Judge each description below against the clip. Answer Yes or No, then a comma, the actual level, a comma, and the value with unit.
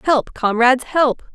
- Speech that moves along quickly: No, slow, 135 wpm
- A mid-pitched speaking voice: No, very high, 255 Hz